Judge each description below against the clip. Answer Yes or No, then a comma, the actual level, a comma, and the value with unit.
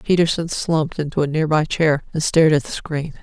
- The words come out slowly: No, fast, 205 wpm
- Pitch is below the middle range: No, medium, 155 Hz